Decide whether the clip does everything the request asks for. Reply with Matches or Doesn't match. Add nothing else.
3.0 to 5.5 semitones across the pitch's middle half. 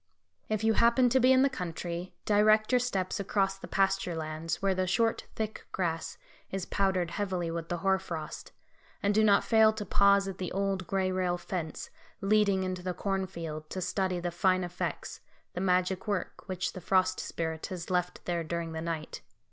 Doesn't match